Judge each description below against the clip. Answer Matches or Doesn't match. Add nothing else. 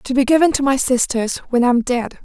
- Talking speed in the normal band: Doesn't match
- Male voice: Doesn't match